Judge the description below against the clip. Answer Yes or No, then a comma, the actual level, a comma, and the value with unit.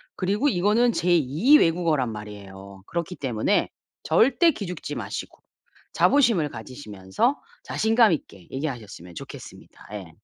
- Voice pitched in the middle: Yes, medium, 155 Hz